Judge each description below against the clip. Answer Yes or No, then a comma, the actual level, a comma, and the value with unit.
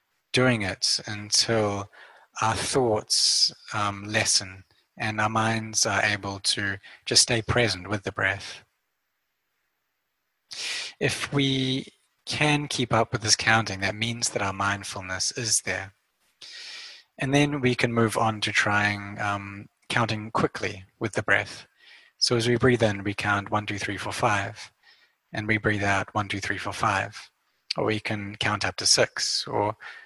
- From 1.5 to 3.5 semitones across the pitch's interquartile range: Yes, average, 2.8 semitones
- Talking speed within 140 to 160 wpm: Yes, average, 155 wpm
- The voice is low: Yes, low, 105 Hz